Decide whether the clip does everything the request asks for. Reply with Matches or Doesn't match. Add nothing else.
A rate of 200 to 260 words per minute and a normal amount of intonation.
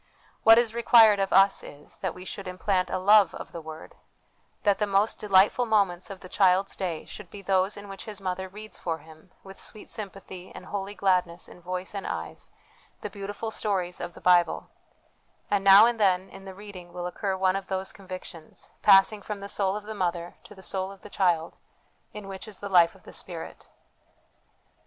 Doesn't match